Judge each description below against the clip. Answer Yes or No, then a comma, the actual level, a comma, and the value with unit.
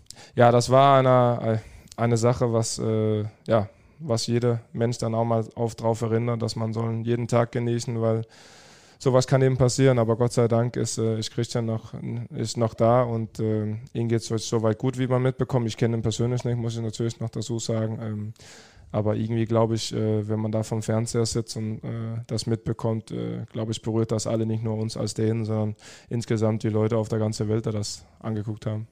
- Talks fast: Yes, fast, 210 wpm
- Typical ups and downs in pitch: No, narrow, 1.3 semitones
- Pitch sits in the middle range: No, low, 115 Hz